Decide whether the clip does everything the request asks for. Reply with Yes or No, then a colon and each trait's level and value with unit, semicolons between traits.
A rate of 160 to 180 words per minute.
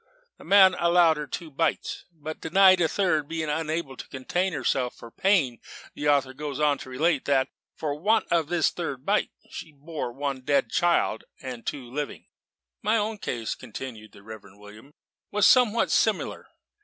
Yes: average, 170 wpm